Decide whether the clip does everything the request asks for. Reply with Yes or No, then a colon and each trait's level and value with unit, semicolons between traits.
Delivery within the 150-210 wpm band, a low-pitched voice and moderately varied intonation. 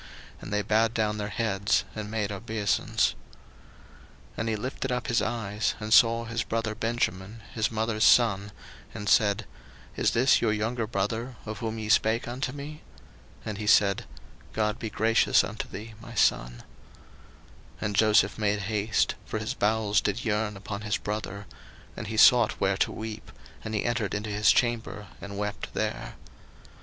No: average, 170 wpm; low, 110 Hz; narrow, 1.8 semitones